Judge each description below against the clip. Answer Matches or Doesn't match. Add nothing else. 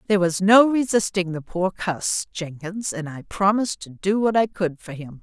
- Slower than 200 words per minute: Doesn't match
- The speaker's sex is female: Matches